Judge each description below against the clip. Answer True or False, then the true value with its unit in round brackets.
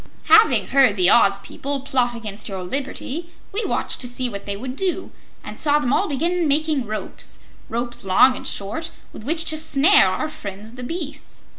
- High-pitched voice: True (265 Hz)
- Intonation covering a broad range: True (6.1 semitones)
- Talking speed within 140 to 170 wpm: False (185 wpm)